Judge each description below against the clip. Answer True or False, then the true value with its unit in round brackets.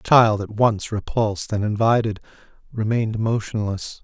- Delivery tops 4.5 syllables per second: True (4.9 syllables/s)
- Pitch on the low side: True (110 Hz)